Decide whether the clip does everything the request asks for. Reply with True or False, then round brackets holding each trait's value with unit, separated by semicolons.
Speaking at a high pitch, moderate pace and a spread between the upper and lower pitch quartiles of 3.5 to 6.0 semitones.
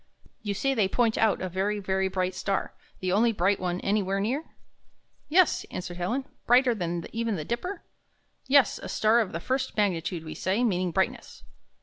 True (200 Hz; 180 wpm; 4.3 semitones)